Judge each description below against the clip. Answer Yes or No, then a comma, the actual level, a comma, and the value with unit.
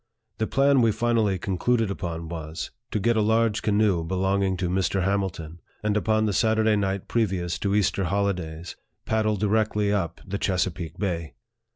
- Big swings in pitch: No, average, 3.3 semitones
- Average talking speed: Yes, average, 165 wpm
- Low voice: Yes, low, 100 Hz